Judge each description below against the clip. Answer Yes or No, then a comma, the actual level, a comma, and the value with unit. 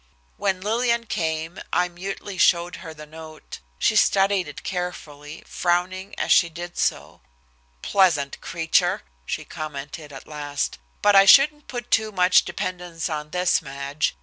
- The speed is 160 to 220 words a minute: No, average, 145 wpm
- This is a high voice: No, medium, 175 Hz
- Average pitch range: Yes, average, 3.9 semitones